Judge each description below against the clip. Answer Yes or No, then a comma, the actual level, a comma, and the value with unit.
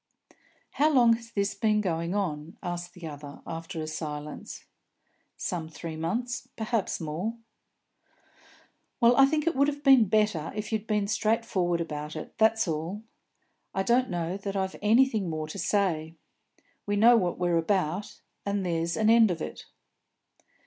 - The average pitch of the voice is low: No, high, 195 Hz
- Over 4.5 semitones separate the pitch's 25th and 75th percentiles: Yes, average, 5.2 semitones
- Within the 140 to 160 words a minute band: Yes, average, 155 wpm